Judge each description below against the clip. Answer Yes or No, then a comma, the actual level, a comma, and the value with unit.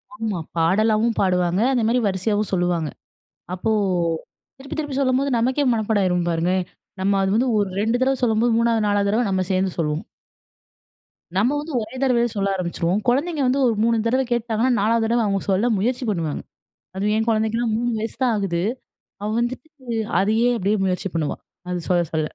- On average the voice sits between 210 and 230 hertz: Yes, high, 215 Hz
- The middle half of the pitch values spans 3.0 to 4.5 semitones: Yes, average, 4.2 semitones